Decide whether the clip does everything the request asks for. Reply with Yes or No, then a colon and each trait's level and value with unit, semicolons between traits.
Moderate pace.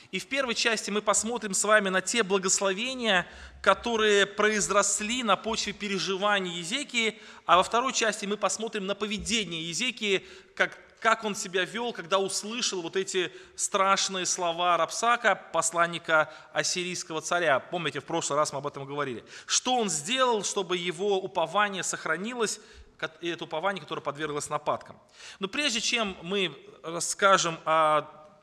Yes: average, 140 wpm